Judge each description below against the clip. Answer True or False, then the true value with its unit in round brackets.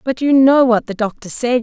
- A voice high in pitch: True (245 Hz)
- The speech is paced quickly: True (260 wpm)